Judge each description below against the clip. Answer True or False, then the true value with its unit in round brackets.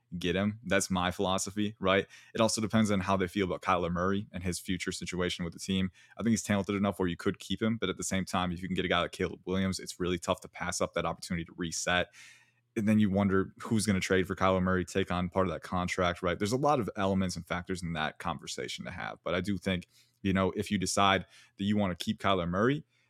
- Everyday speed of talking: False (270 wpm)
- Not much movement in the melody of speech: True (2.0 semitones)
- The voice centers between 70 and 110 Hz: True (95 Hz)